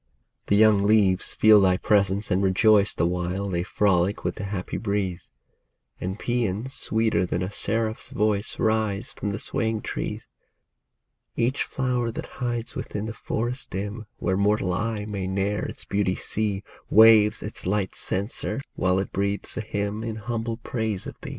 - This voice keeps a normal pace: Yes, average, 165 wpm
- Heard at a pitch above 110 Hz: No, low, 105 Hz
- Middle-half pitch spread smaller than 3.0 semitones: Yes, narrow, 2.4 semitones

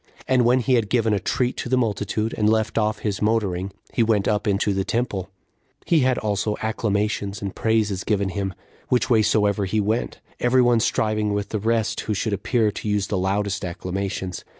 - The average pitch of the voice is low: Yes, low, 105 Hz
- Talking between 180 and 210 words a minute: Yes, average, 195 wpm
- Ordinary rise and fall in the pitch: No, narrow, 2.2 semitones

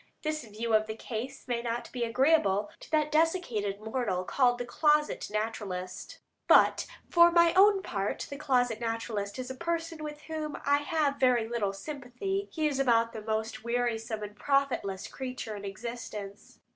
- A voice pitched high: Yes, high, 245 Hz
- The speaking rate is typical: Yes, average, 165 wpm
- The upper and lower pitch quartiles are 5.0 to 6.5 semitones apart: Yes, wide, 5.5 semitones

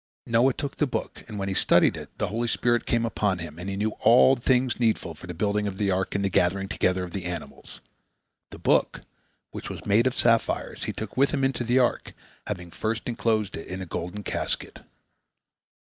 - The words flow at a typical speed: No, fast, 210 wpm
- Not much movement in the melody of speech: No, average, 4.2 semitones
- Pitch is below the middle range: Yes, low, 105 Hz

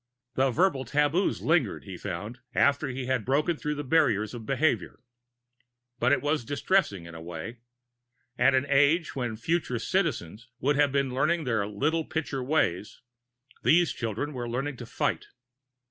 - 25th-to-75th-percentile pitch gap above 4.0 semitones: Yes, average, 4.5 semitones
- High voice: No, low, 135 Hz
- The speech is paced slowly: No, average, 160 wpm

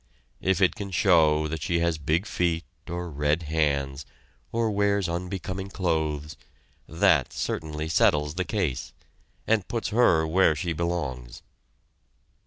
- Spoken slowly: Yes, slow, 130 wpm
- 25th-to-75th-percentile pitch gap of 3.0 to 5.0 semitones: Yes, average, 3.7 semitones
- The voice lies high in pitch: No, very low, 85 Hz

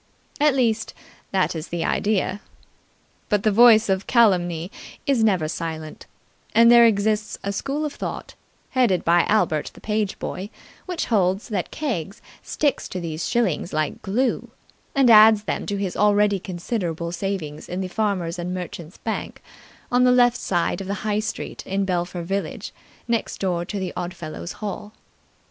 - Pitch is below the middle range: No, high, 200 Hz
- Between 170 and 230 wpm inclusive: No, average, 160 wpm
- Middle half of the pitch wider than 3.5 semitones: Yes, average, 4.0 semitones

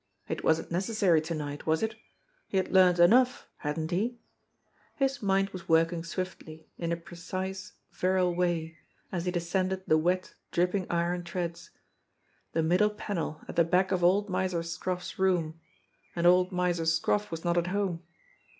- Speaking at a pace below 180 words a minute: Yes, average, 160 wpm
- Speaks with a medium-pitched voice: Yes, medium, 180 Hz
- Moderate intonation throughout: No, narrow, 2.1 semitones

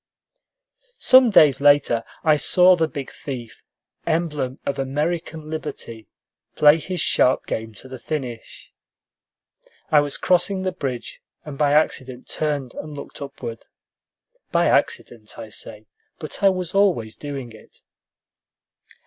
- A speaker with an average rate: No, slow, 130 wpm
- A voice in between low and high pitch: Yes, medium, 145 Hz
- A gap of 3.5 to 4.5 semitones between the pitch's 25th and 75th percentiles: Yes, average, 4.2 semitones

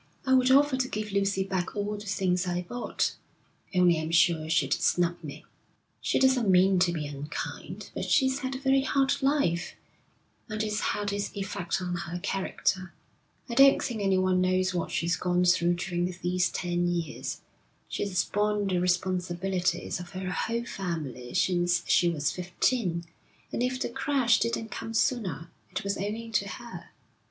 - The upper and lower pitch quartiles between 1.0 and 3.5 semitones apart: No, average, 4.0 semitones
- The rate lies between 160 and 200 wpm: Yes, average, 165 wpm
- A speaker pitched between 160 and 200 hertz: Yes, medium, 185 Hz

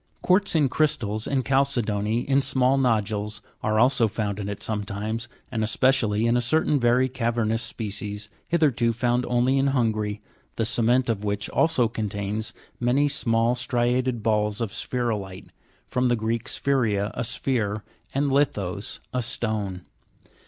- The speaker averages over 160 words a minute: No, average, 145 wpm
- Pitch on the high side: No, low, 115 Hz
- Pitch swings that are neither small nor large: Yes, average, 3.3 semitones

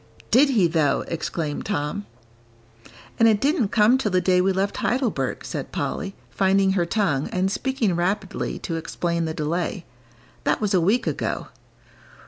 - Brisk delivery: No, average, 155 wpm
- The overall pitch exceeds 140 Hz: Yes, high, 190 Hz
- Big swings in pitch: No, average, 3.9 semitones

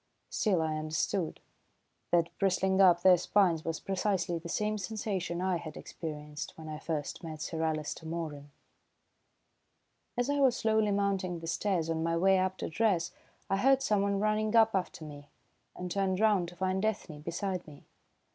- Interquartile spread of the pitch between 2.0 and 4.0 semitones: Yes, average, 3.7 semitones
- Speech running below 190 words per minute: Yes, average, 165 wpm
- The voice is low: No, medium, 180 Hz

